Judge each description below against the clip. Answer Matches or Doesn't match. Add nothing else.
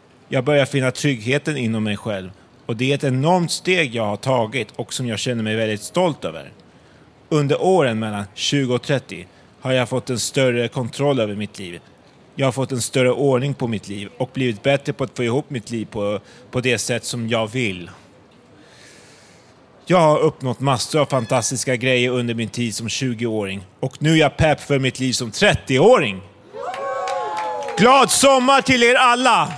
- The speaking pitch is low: Matches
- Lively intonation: Doesn't match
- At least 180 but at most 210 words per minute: Matches